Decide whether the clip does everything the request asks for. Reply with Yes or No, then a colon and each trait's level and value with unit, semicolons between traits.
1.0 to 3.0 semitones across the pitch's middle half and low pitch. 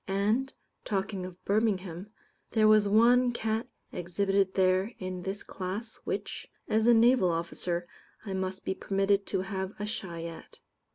No: average, 2.7 semitones; high, 195 Hz